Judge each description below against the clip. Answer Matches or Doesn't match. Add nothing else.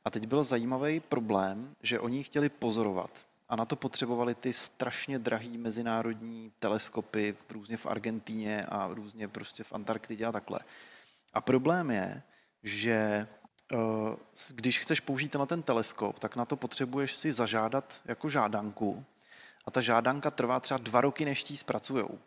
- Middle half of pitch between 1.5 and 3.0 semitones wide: Doesn't match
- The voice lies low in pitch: Matches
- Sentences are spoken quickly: Doesn't match